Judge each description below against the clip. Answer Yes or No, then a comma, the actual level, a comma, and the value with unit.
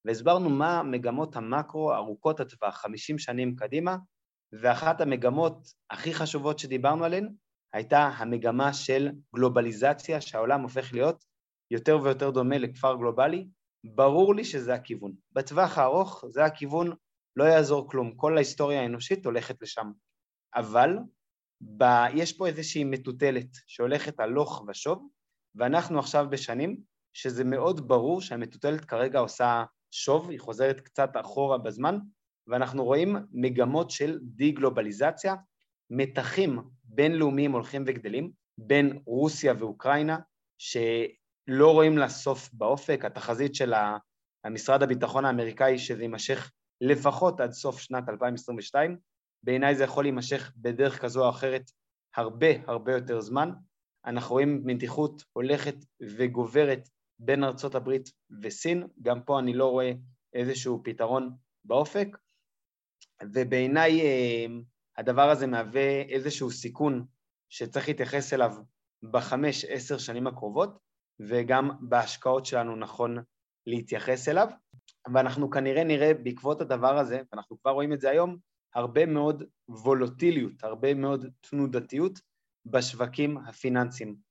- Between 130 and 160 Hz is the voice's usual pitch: Yes, low, 135 Hz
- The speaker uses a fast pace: No, average, 115 wpm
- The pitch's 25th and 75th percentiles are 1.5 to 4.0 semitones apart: Yes, average, 3.2 semitones